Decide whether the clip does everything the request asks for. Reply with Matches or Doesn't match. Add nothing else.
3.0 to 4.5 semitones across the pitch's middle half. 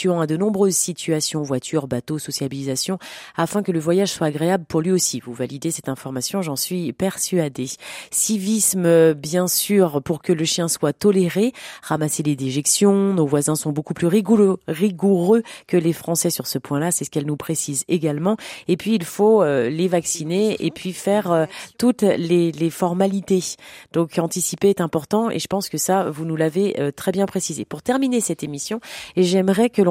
Matches